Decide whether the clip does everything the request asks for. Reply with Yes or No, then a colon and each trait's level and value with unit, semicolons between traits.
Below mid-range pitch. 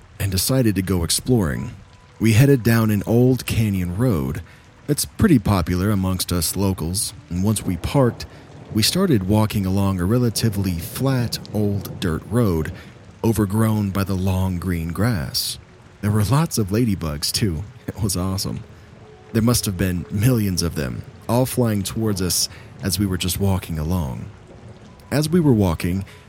Yes: low, 105 Hz